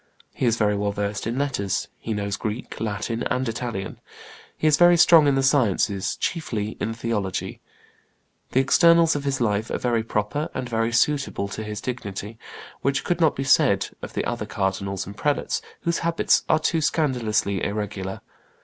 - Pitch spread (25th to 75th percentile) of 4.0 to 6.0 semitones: Yes, wide, 5.5 semitones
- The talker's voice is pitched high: No, low, 115 Hz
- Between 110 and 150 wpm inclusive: No, average, 175 wpm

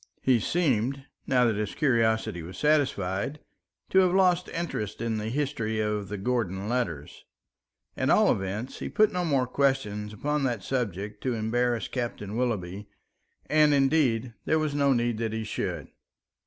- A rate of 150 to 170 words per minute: Yes, average, 155 wpm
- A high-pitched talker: No, low, 120 Hz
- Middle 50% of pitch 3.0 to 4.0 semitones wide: No, average, 4.8 semitones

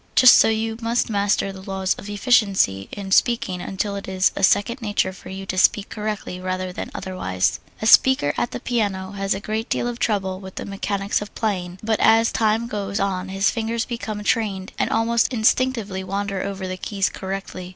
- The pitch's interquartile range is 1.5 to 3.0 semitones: Yes, average, 2.7 semitones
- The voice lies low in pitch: No, high, 200 Hz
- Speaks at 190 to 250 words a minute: Yes, average, 195 wpm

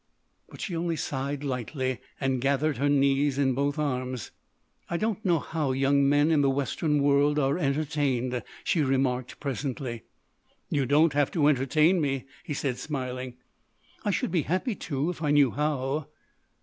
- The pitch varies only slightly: Yes, narrow, 2.3 semitones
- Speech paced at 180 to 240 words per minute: No, average, 160 wpm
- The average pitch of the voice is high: No, medium, 140 Hz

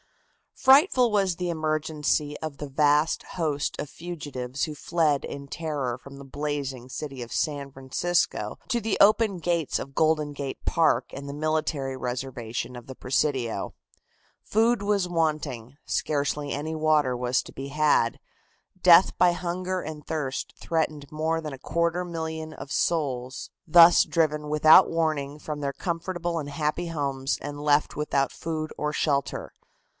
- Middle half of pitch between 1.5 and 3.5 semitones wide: Yes, average, 3.1 semitones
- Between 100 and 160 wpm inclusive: Yes, average, 150 wpm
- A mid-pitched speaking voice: Yes, medium, 150 Hz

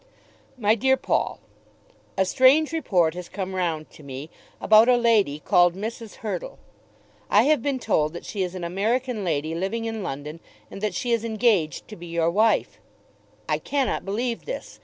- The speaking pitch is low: No, high, 205 Hz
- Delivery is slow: No, average, 175 wpm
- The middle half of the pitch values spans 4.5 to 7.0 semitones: Yes, wide, 5.5 semitones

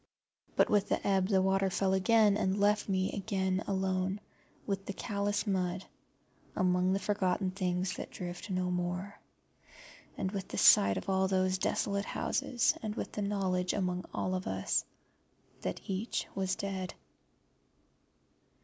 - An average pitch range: No, narrow, 1.5 semitones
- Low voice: No, high, 190 Hz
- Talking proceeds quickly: No, average, 150 wpm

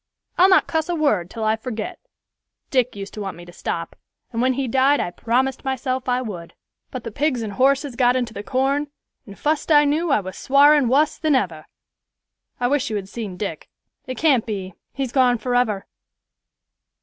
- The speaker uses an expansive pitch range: No, average, 4.7 semitones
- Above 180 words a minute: Yes, average, 195 wpm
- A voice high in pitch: Yes, very high, 250 Hz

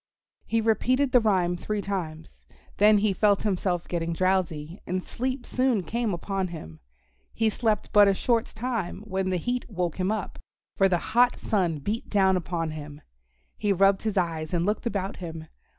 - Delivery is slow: No, average, 175 wpm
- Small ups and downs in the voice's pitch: No, average, 3.9 semitones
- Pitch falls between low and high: No, high, 195 Hz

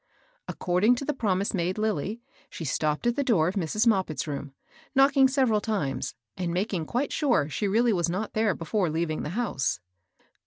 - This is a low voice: No, high, 200 Hz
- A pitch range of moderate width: No, wide, 5.9 semitones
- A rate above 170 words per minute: Yes, average, 185 wpm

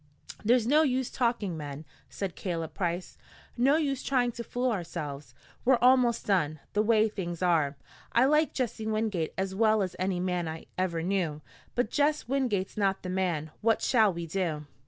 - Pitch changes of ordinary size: No, wide, 5.9 semitones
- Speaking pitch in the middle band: No, high, 195 Hz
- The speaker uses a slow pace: No, average, 175 wpm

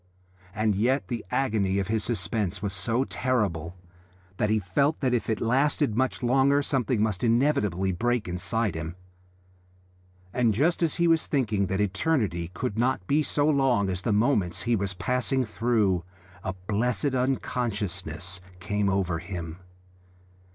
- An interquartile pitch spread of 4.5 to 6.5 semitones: Yes, average, 5.1 semitones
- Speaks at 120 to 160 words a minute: Yes, average, 150 wpm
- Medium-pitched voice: No, low, 110 Hz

